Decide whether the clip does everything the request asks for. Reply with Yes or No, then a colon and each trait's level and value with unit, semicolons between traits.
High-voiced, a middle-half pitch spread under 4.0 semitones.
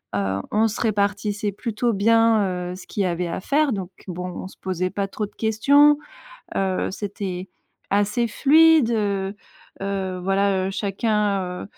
Yes: high, 200 Hz; average, 2.8 semitones